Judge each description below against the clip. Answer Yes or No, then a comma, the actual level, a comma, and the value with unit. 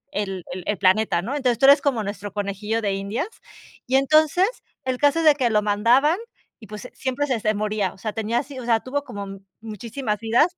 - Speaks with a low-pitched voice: No, high, 225 Hz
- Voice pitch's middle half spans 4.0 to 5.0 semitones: Yes, average, 4.7 semitones